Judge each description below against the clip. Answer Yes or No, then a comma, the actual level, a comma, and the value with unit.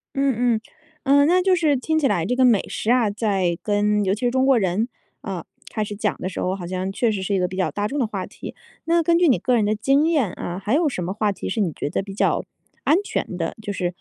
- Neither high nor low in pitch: No, high, 215 Hz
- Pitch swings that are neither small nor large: No, wide, 6.0 semitones